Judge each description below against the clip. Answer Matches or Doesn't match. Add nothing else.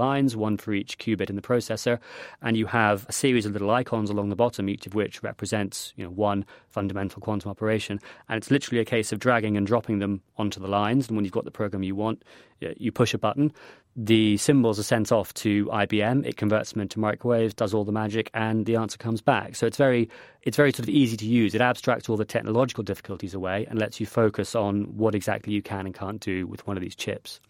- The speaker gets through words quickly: Matches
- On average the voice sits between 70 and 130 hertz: Matches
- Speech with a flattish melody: Matches